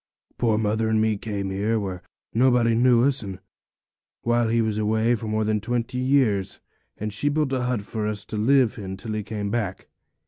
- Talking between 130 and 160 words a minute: No, average, 195 wpm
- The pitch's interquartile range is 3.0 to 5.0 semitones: No, narrow, 2.4 semitones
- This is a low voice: Yes, low, 110 Hz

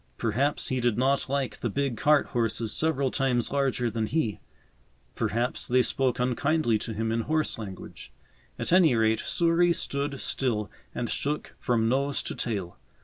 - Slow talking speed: No, average, 160 wpm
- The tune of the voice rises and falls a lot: No, average, 3.7 semitones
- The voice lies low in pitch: Yes, low, 125 Hz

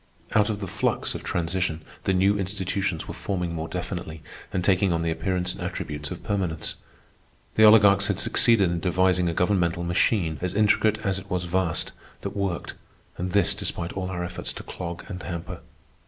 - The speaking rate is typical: Yes, average, 180 wpm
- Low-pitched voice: Yes, very low, 90 Hz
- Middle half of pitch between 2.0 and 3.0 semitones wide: Yes, narrow, 2.4 semitones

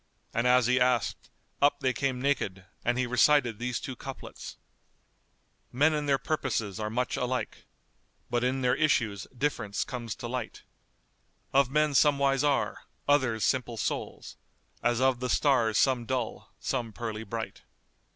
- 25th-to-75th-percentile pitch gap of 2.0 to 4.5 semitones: Yes, average, 2.8 semitones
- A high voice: No, low, 125 Hz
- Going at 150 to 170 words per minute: Yes, average, 160 wpm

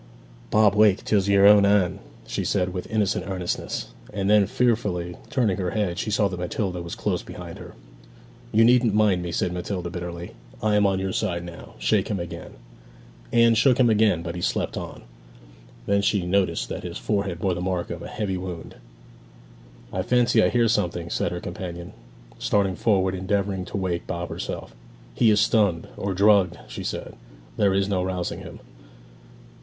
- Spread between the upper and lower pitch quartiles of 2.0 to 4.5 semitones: Yes, average, 2.9 semitones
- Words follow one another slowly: No, average, 180 wpm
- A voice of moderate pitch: No, very low, 95 Hz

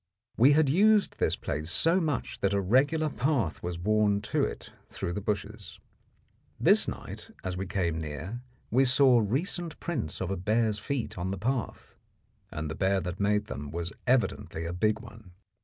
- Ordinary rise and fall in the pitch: No, wide, 6.6 semitones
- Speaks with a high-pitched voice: No, low, 105 Hz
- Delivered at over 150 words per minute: Yes, average, 175 wpm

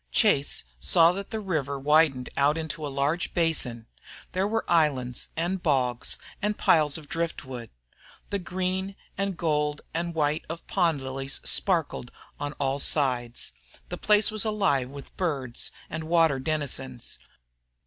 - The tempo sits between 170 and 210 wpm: No, average, 140 wpm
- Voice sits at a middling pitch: Yes, medium, 155 Hz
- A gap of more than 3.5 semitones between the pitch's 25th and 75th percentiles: Yes, average, 4.4 semitones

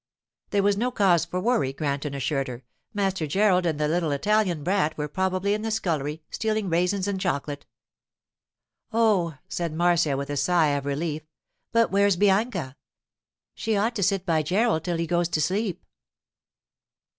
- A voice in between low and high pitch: Yes, medium, 175 Hz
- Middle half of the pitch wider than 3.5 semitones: Yes, average, 4.9 semitones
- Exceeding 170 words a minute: No, average, 165 wpm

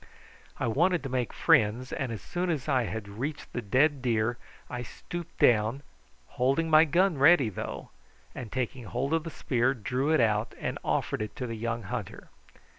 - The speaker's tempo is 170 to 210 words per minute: Yes, average, 180 wpm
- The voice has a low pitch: Yes, low, 125 Hz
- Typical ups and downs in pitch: Yes, average, 4.7 semitones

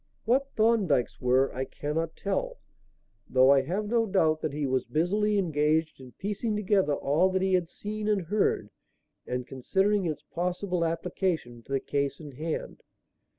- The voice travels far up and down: Yes, wide, 6.2 semitones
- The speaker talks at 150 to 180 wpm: Yes, average, 160 wpm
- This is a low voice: No, medium, 165 Hz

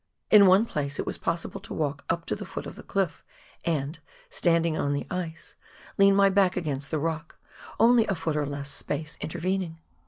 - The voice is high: No, medium, 165 Hz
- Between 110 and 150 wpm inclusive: No, average, 195 wpm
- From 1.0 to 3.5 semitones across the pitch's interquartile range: No, average, 4.0 semitones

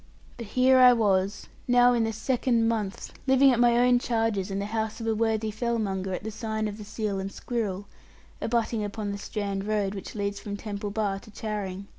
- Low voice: No, high, 215 Hz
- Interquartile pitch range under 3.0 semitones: Yes, narrow, 2.4 semitones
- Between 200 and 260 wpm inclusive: Yes, fast, 205 wpm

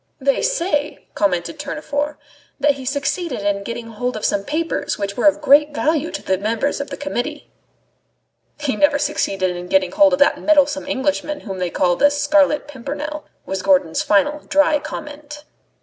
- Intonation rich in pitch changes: Yes, wide, 6.1 semitones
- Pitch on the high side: Yes, very high, 285 Hz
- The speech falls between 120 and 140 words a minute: No, average, 170 wpm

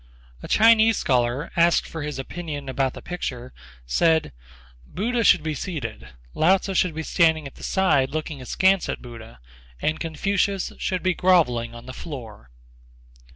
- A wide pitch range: Yes, wide, 6.0 semitones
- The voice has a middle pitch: Yes, medium, 155 Hz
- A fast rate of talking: No, average, 155 wpm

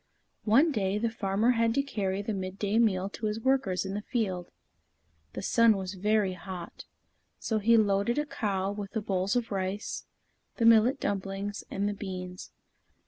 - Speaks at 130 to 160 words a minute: No, average, 170 wpm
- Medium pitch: No, high, 205 Hz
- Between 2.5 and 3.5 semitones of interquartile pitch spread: Yes, average, 2.9 semitones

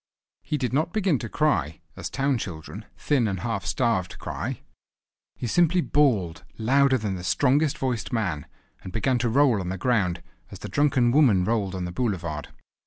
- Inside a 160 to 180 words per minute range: Yes, average, 175 wpm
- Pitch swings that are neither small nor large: No, wide, 6.7 semitones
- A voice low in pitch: Yes, low, 115 Hz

